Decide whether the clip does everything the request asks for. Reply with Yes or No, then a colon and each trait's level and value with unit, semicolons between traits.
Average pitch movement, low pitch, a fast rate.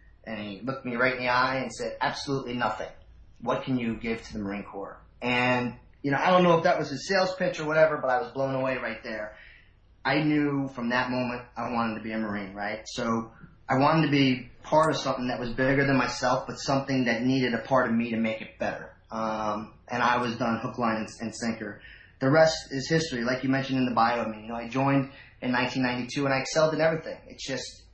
Yes: average, 3.3 semitones; low, 125 Hz; fast, 245 wpm